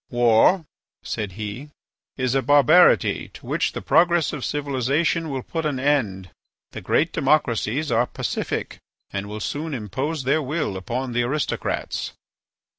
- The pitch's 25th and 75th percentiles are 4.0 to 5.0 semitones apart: Yes, average, 4.5 semitones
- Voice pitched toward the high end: No, low, 135 Hz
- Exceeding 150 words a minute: No, average, 140 wpm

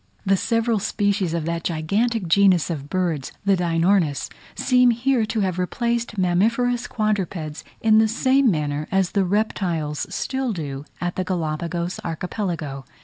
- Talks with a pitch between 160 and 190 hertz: Yes, medium, 185 Hz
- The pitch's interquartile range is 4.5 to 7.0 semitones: Yes, average, 4.9 semitones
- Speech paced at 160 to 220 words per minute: No, average, 145 wpm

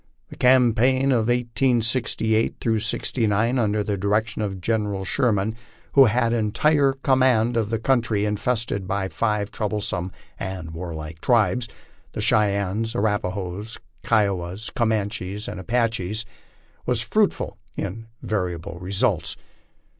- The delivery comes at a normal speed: No, slow, 115 wpm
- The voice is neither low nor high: No, low, 110 Hz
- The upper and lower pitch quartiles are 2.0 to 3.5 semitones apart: Yes, average, 2.9 semitones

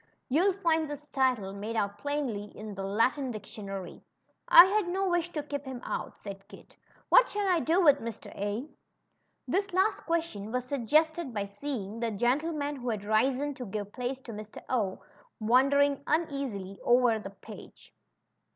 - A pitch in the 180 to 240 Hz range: No, very high, 255 Hz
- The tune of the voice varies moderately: No, wide, 6.3 semitones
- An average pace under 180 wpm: Yes, average, 160 wpm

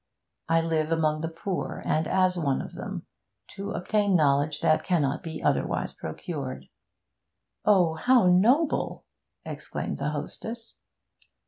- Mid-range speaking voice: Yes, medium, 165 Hz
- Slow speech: Yes, slow, 125 wpm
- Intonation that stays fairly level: No, average, 3.8 semitones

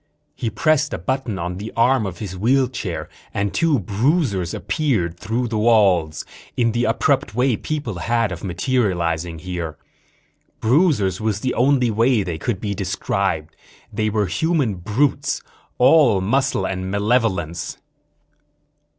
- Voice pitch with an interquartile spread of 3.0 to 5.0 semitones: No, wide, 5.5 semitones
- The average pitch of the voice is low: Yes, low, 110 Hz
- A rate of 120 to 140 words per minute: Yes, slow, 135 wpm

